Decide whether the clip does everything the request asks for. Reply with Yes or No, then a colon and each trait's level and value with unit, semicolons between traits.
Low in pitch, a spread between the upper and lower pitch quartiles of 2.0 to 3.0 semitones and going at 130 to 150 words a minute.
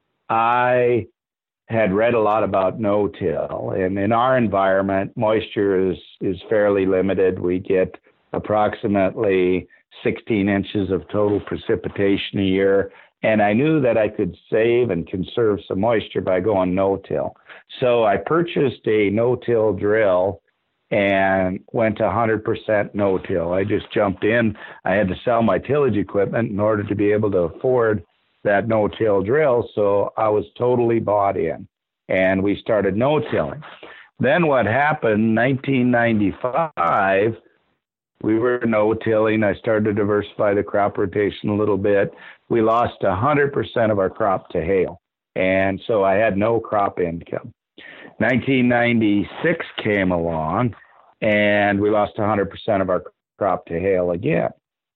Yes: low, 105 Hz; narrow, 2.6 semitones; average, 145 wpm